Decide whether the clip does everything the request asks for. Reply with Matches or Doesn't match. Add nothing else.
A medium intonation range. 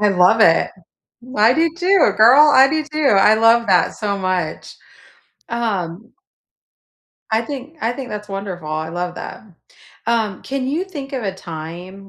Doesn't match